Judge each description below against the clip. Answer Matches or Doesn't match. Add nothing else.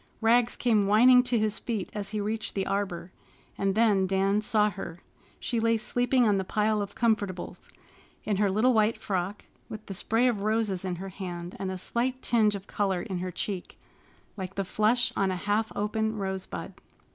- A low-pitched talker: Doesn't match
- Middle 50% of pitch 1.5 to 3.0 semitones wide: Matches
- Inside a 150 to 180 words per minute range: Doesn't match